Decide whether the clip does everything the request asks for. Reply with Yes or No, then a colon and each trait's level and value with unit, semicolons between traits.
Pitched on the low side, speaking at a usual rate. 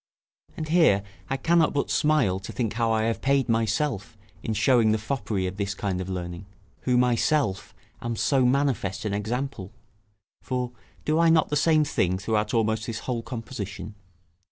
Yes: low, 115 Hz; average, 170 wpm